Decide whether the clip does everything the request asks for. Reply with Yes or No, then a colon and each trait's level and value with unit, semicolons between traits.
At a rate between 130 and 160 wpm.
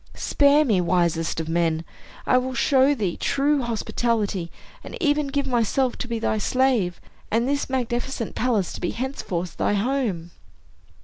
Yes: average, 150 wpm